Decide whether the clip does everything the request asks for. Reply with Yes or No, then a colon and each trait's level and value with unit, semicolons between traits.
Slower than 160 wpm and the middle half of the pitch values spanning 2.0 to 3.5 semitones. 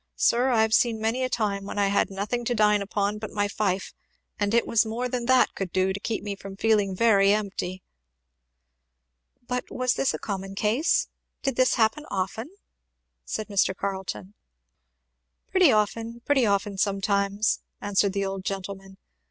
No: average, 170 wpm; average, 2.9 semitones